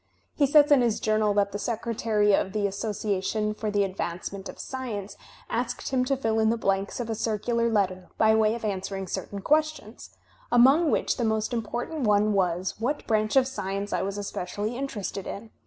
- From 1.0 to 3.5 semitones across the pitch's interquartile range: Yes, average, 3.0 semitones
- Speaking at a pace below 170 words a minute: No, average, 190 wpm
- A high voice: Yes, high, 215 Hz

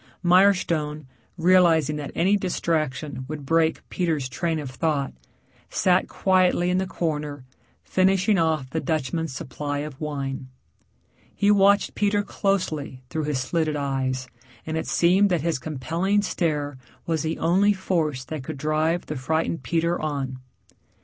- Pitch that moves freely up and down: No, average, 3.8 semitones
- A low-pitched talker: No, medium, 160 Hz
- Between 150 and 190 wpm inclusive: No, average, 140 wpm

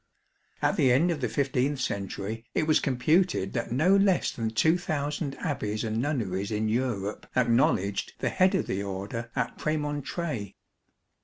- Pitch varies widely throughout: Yes, wide, 6.1 semitones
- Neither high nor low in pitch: No, low, 125 Hz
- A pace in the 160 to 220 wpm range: No, average, 150 wpm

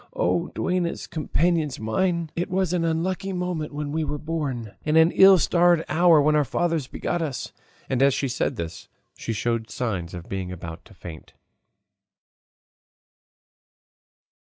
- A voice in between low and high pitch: Yes, medium, 155 Hz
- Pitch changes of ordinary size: No, wide, 6.3 semitones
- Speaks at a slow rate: No, average, 150 wpm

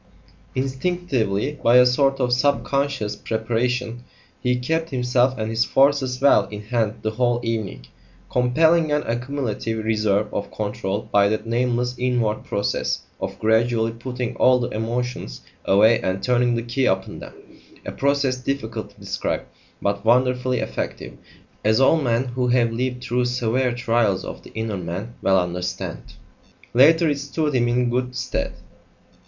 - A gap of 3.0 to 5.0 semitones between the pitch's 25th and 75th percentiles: No, narrow, 2.6 semitones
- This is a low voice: Yes, low, 120 Hz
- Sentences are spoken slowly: No, average, 150 wpm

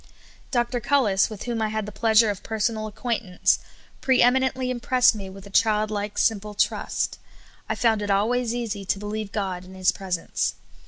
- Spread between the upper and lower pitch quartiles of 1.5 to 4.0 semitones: Yes, average, 3.0 semitones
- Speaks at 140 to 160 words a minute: No, average, 190 wpm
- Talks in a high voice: Yes, high, 215 Hz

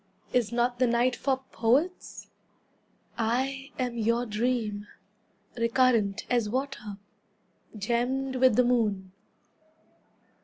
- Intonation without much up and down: Yes, narrow, 2.3 semitones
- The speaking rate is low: Yes, slow, 100 wpm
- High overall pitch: Yes, high, 240 Hz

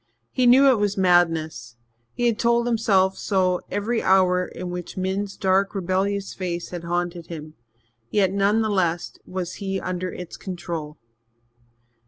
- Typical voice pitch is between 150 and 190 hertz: Yes, medium, 185 Hz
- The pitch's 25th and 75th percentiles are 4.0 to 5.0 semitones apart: No, narrow, 2.4 semitones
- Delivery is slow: No, average, 150 wpm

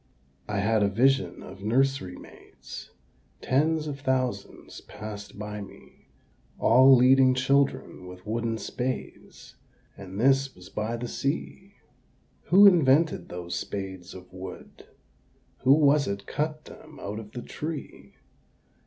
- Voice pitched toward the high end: No, low, 125 Hz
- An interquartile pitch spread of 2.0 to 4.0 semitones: No, average, 5.2 semitones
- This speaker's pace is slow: Yes, slow, 125 wpm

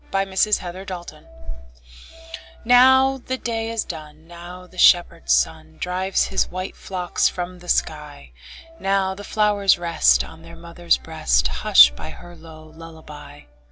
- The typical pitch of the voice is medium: Yes, medium, 175 Hz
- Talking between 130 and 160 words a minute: Yes, average, 145 wpm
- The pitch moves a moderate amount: Yes, average, 3.5 semitones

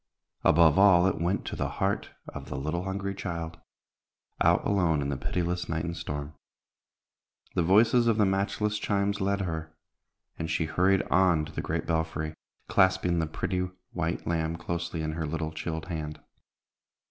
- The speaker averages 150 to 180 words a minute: Yes, average, 165 wpm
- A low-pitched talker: Yes, very low, 85 Hz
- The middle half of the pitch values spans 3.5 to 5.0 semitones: No, average, 3.1 semitones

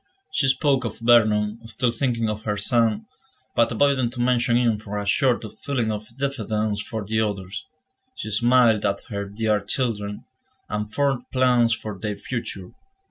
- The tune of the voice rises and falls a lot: No, average, 2.8 semitones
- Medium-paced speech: Yes, average, 165 wpm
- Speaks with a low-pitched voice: Yes, low, 110 Hz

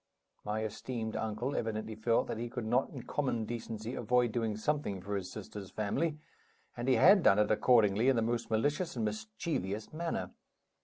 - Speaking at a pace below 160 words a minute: No, average, 175 wpm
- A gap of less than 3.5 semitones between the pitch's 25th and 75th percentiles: Yes, average, 2.7 semitones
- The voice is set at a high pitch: No, low, 115 Hz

